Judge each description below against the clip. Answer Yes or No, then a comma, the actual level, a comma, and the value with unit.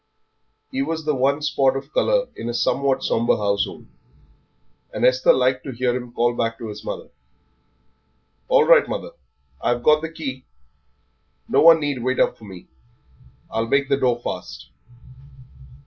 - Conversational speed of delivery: Yes, average, 160 wpm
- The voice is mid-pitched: No, low, 130 Hz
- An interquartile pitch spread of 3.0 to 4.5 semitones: Yes, average, 3.5 semitones